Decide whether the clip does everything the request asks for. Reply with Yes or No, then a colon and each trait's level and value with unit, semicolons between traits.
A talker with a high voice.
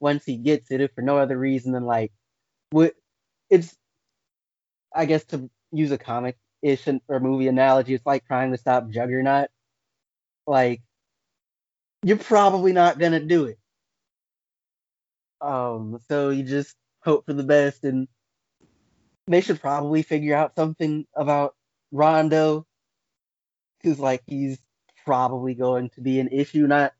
No: medium, 140 Hz